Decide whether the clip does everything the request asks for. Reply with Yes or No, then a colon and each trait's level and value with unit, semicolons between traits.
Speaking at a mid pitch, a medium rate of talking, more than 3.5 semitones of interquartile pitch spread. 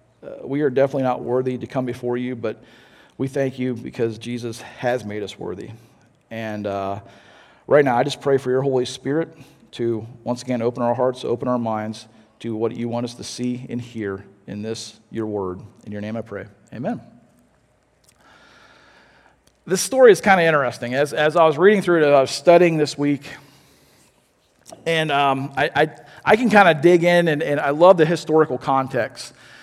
No: low, 125 Hz; average, 190 wpm; average, 4.0 semitones